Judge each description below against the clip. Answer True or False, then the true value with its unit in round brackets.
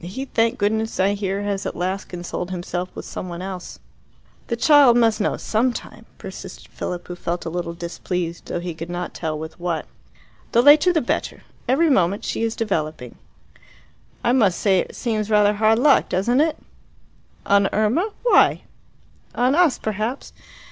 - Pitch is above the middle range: True (205 Hz)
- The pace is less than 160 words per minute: False (170 wpm)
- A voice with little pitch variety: False (4.8 semitones)